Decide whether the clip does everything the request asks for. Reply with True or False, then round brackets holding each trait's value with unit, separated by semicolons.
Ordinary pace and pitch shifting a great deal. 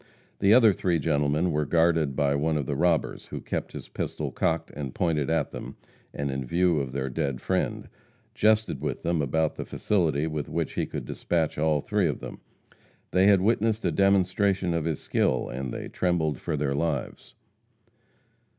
False (180 wpm; 4.0 semitones)